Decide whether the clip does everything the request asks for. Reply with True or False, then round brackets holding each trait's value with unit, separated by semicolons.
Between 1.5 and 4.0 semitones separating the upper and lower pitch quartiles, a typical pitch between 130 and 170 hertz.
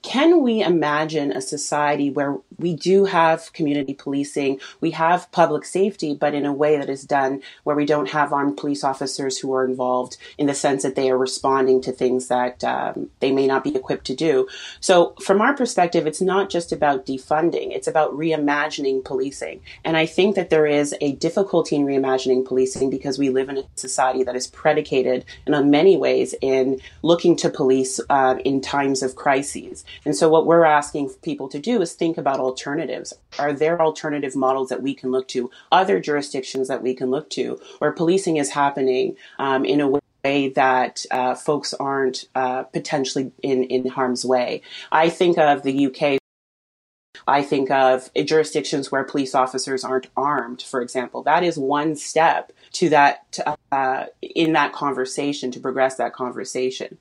True (2.9 semitones; 140 Hz)